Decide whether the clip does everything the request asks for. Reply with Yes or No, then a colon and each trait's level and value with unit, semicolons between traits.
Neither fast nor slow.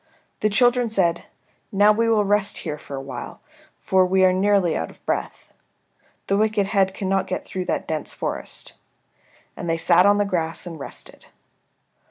Yes: average, 175 wpm